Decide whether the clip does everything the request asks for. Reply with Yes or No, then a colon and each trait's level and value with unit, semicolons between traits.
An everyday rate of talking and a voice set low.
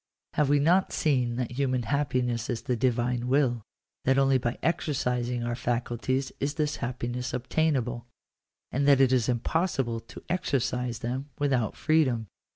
Yes: average, 160 wpm; low, 125 Hz